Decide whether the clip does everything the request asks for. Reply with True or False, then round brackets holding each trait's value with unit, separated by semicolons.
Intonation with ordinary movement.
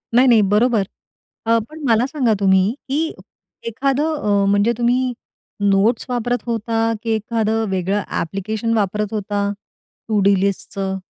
True (3.2 semitones)